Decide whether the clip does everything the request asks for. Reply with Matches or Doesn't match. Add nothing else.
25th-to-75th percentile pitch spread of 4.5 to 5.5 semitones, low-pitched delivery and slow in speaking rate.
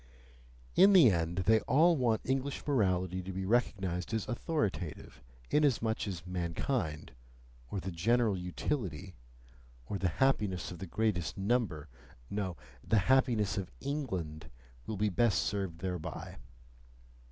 Matches